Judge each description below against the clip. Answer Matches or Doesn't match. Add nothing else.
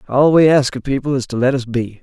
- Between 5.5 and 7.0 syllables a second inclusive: Matches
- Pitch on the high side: Doesn't match